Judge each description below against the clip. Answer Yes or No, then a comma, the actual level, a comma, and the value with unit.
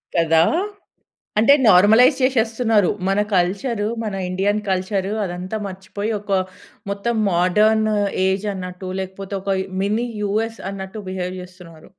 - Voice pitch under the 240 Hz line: Yes, high, 195 Hz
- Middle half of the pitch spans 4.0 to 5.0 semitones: No, average, 2.8 semitones